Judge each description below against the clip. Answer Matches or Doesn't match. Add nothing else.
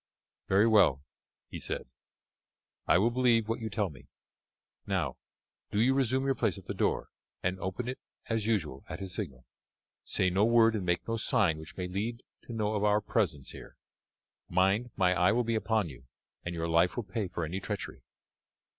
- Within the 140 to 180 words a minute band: Doesn't match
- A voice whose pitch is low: Matches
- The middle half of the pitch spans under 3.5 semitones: Doesn't match